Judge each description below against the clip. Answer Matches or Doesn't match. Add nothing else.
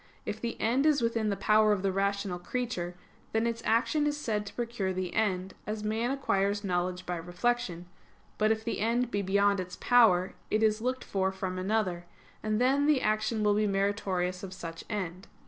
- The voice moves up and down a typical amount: Matches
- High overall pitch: Matches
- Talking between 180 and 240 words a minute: Matches